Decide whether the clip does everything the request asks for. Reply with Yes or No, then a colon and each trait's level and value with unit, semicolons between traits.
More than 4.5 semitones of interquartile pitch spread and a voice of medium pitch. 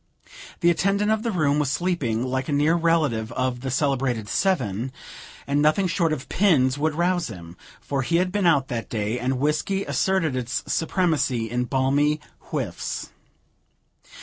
Yes: average, 5.3 semitones; medium, 145 Hz